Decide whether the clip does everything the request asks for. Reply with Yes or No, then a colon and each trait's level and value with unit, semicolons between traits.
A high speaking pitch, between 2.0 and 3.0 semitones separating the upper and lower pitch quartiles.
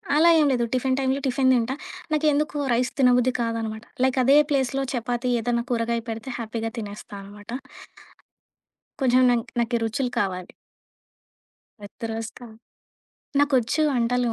Yes: high, 245 Hz; narrow, 2.6 semitones